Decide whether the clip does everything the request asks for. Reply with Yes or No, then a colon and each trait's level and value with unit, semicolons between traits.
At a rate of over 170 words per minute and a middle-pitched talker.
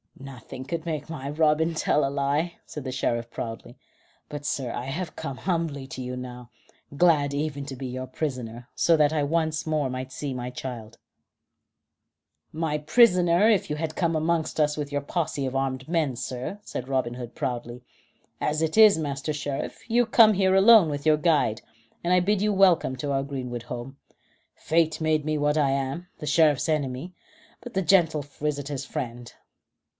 Yes: average, 180 wpm; medium, 145 Hz